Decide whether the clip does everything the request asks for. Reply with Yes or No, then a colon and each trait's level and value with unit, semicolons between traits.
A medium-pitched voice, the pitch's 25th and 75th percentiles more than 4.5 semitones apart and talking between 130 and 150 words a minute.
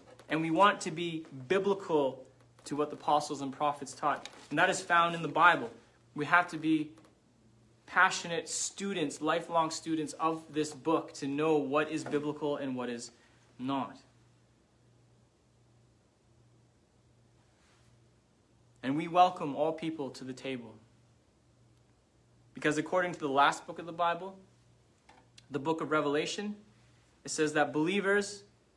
Yes: medium, 150 Hz; average, 5.1 semitones; slow, 135 wpm